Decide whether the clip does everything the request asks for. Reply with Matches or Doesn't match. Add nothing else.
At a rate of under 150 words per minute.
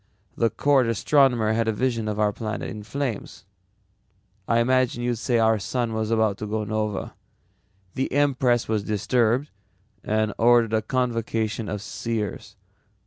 Matches